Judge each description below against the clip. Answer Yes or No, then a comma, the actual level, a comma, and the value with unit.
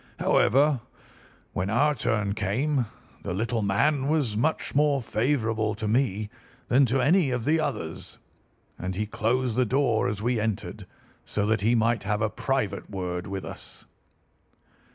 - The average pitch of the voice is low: Yes, low, 115 Hz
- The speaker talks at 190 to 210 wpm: No, average, 155 wpm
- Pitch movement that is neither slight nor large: Yes, average, 4.4 semitones